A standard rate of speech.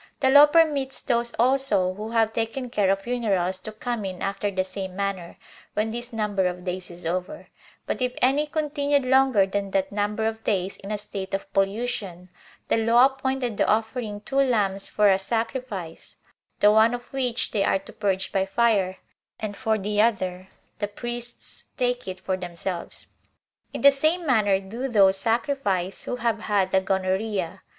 Yes: average, 175 wpm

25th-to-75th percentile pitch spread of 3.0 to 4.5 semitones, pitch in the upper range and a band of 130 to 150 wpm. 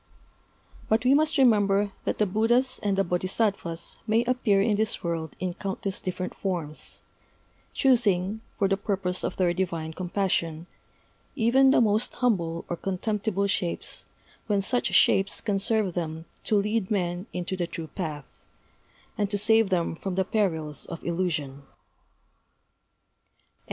Yes: average, 3.8 semitones; high, 195 Hz; average, 140 wpm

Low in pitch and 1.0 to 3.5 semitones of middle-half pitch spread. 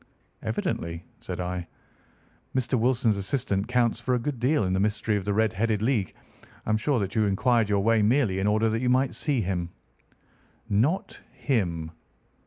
No: low, 110 Hz; average, 4.0 semitones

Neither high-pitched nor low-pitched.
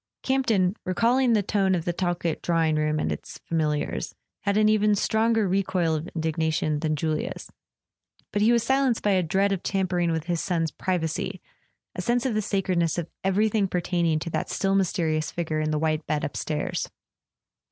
Yes: medium, 180 Hz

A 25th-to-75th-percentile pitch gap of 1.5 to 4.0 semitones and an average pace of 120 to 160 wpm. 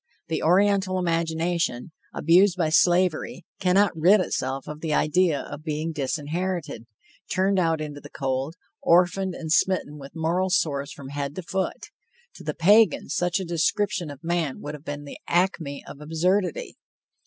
Yes: average, 3.6 semitones; average, 155 wpm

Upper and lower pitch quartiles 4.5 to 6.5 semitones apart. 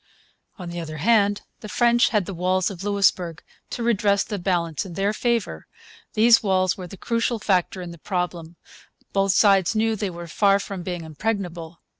No: average, 3.2 semitones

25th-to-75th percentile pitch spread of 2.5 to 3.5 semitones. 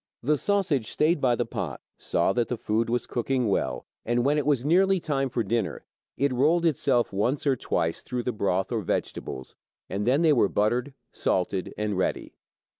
No: average, 5.1 semitones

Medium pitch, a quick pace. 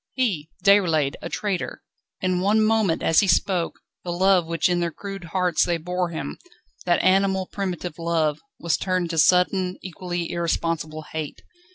No: medium, 175 Hz; average, 160 wpm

